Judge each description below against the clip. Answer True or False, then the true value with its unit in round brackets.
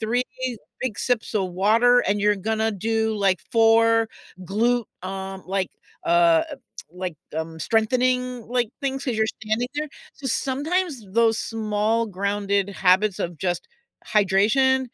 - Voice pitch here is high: True (220 Hz)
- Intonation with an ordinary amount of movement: True (4.0 semitones)